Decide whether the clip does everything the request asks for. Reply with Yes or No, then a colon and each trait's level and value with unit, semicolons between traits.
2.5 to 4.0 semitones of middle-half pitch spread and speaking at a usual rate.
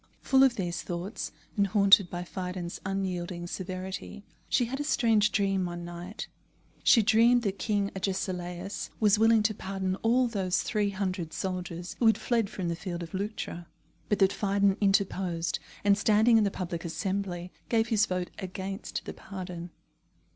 Yes: average, 2.8 semitones; average, 160 wpm